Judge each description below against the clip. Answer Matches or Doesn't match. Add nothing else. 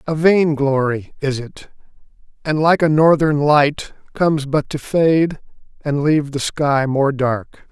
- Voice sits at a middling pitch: Matches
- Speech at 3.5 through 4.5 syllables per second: Matches